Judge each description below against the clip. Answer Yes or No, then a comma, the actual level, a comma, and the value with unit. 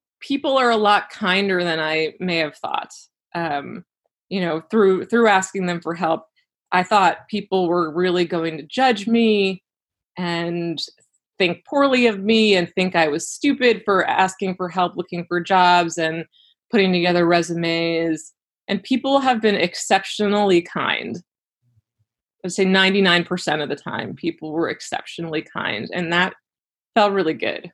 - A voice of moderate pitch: Yes, medium, 180 Hz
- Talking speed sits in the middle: Yes, average, 155 wpm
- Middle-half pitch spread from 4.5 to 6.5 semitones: No, average, 3.6 semitones